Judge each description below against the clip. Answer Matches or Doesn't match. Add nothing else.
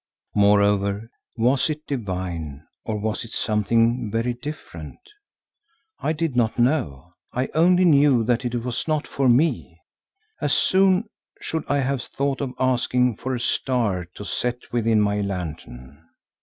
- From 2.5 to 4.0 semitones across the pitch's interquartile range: Doesn't match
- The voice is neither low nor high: Doesn't match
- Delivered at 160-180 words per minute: Doesn't match